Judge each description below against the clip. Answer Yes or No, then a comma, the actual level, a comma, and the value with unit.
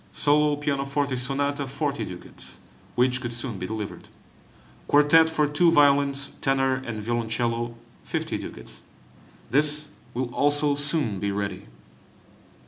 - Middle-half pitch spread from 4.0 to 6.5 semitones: No, average, 3.6 semitones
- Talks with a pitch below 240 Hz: Yes, medium, 140 Hz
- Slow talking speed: Yes, slow, 120 wpm